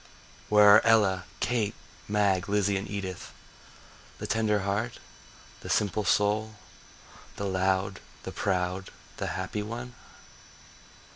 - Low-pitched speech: Yes, low, 100 Hz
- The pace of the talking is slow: Yes, slow, 115 wpm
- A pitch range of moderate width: No, narrow, 1.9 semitones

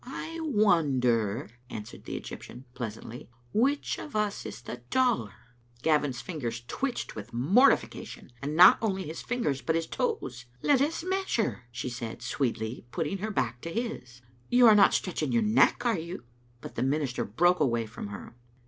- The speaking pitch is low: No, medium, 155 Hz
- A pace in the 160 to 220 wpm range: Yes, average, 170 wpm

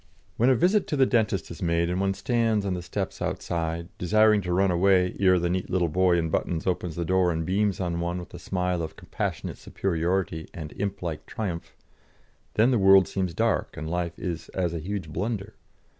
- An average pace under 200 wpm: No, fast, 205 wpm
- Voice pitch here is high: No, very low, 90 Hz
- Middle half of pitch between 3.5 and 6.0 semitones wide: No, average, 2.7 semitones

